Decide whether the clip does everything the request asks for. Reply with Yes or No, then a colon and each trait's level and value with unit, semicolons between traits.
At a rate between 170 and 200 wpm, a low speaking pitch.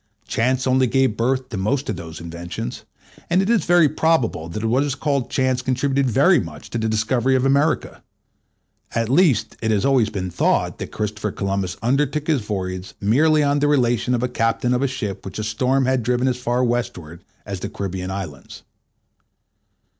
Yes: average, 185 wpm; low, 125 Hz